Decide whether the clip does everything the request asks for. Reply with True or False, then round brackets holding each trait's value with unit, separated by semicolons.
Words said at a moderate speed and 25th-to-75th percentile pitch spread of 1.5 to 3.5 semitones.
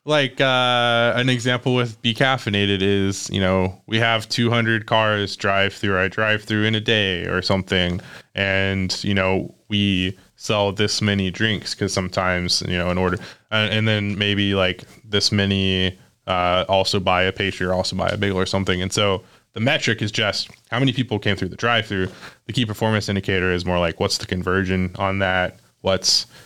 True (190 wpm; 2.9 semitones)